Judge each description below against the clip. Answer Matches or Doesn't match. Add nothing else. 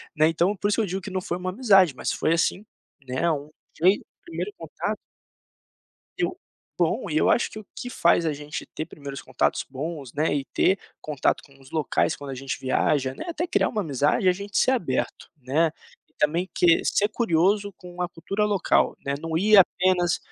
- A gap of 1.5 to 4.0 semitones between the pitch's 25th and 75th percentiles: Doesn't match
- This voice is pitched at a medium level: Matches